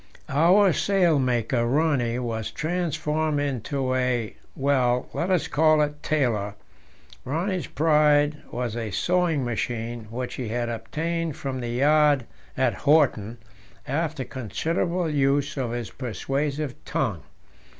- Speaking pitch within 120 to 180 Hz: Yes, medium, 140 Hz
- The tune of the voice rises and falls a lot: No, average, 4.3 semitones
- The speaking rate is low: Yes, slow, 120 wpm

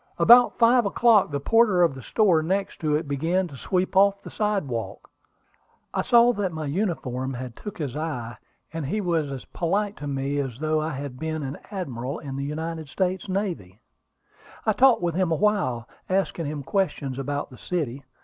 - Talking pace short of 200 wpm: Yes, average, 180 wpm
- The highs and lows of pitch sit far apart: Yes, wide, 5.8 semitones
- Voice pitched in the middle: Yes, medium, 160 Hz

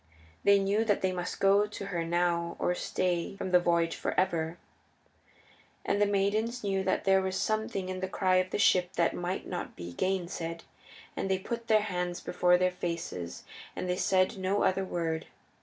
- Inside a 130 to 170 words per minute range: No, average, 190 wpm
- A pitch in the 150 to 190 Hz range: Yes, medium, 185 Hz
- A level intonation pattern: Yes, narrow, 2.0 semitones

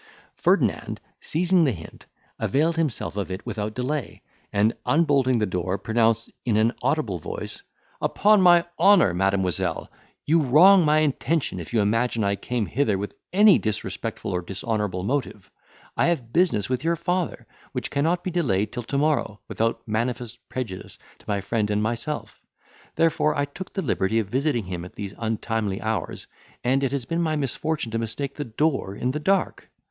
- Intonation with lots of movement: Yes, wide, 6.5 semitones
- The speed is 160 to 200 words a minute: Yes, average, 170 wpm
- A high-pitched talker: No, low, 120 Hz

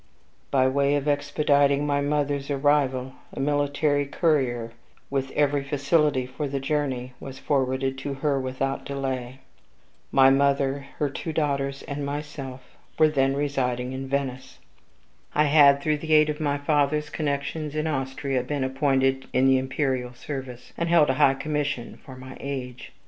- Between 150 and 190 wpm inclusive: Yes, average, 155 wpm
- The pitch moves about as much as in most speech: No, narrow, 1.7 semitones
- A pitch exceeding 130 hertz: Yes, medium, 140 Hz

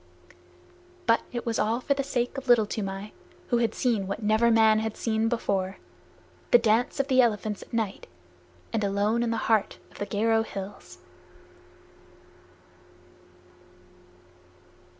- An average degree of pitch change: No, narrow, 2.3 semitones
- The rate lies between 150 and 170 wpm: No, average, 140 wpm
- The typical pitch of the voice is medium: No, high, 225 Hz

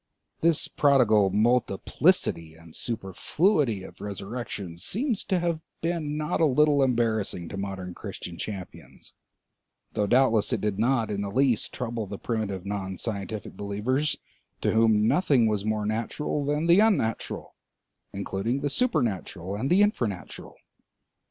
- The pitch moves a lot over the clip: Yes, wide, 6.2 semitones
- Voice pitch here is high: No, low, 110 Hz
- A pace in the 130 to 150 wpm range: Yes, slow, 135 wpm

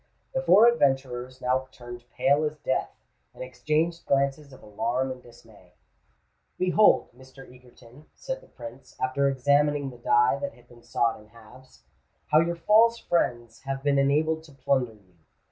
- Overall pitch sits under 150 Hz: Yes, low, 135 Hz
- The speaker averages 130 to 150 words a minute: No, average, 160 wpm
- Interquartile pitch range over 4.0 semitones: No, average, 3.6 semitones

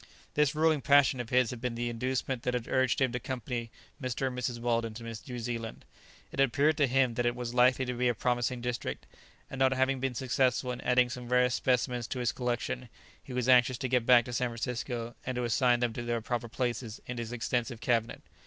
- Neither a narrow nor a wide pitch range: No, narrow, 1.4 semitones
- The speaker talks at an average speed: No, fast, 225 wpm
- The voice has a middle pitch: No, low, 125 Hz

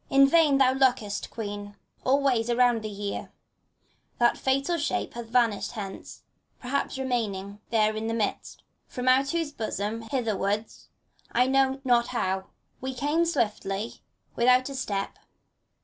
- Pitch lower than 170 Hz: No, high, 240 Hz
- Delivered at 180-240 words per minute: No, average, 155 wpm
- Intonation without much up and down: No, average, 3.9 semitones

